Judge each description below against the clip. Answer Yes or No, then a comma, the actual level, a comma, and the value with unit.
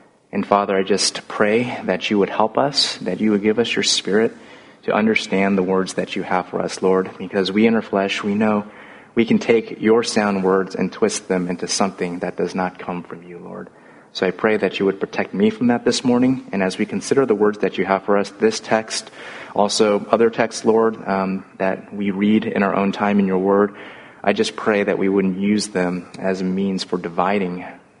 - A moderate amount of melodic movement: No, narrow, 2.0 semitones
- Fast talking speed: Yes, fast, 225 wpm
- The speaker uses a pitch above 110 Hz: No, low, 100 Hz